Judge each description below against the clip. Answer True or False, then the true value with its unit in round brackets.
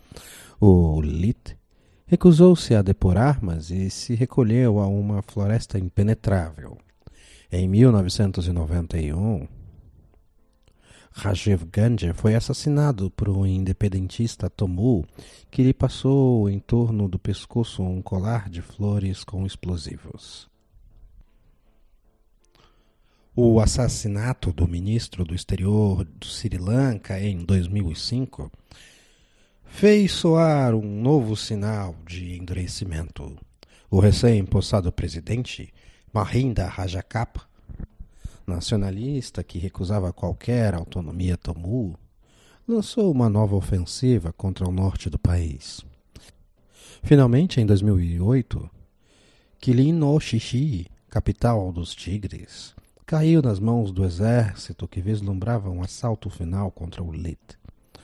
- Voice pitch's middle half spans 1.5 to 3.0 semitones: False (4.3 semitones)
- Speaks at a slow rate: True (100 wpm)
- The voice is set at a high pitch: False (100 Hz)